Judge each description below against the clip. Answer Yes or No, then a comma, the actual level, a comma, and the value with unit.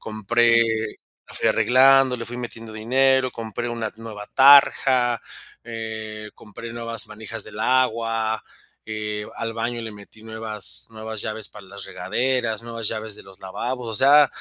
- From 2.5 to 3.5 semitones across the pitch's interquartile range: No, narrow, 1.9 semitones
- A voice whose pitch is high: No, low, 115 Hz